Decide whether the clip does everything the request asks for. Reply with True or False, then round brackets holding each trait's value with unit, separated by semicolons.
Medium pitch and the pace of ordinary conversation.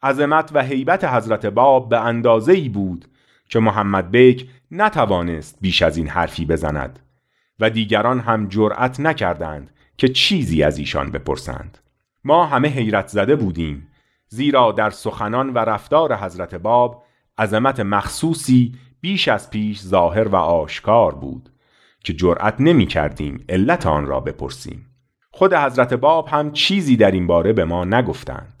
False (115 Hz; 145 wpm)